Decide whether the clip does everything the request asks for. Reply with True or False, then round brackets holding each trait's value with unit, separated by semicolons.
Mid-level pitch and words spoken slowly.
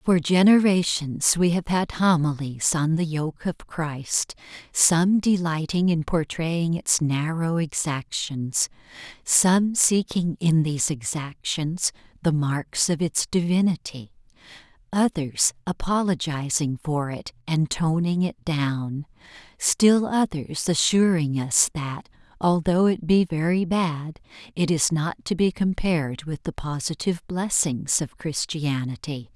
True (165 Hz; 115 wpm)